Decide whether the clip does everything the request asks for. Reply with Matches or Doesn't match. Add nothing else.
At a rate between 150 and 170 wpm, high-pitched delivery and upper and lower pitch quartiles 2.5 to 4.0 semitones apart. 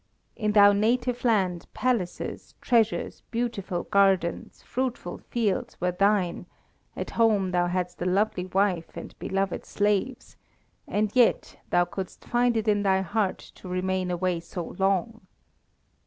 Doesn't match